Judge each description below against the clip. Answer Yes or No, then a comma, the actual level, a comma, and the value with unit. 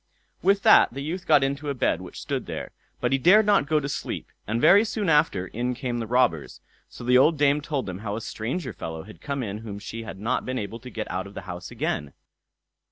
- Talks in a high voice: No, low, 125 Hz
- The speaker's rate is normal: No, fast, 240 wpm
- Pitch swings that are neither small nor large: No, wide, 5.8 semitones